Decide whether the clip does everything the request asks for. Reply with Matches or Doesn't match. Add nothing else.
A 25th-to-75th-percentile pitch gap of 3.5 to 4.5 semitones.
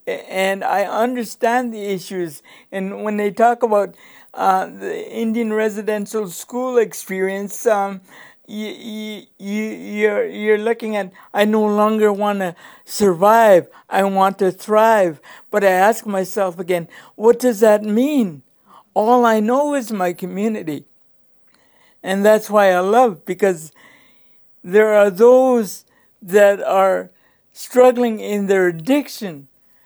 Doesn't match